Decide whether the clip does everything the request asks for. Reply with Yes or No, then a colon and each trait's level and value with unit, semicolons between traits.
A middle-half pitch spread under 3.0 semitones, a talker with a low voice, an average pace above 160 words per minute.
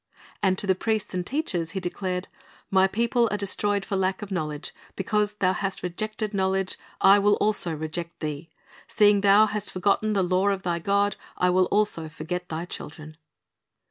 No: narrow, 2.5 semitones; high, 190 Hz; average, 180 wpm